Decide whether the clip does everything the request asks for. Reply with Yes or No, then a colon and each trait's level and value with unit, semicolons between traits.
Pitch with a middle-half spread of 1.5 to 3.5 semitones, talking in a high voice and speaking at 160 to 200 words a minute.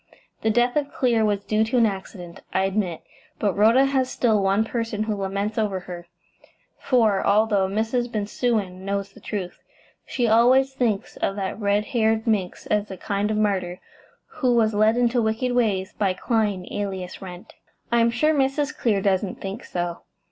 Yes: average, 3.2 semitones; high, 215 Hz; average, 175 wpm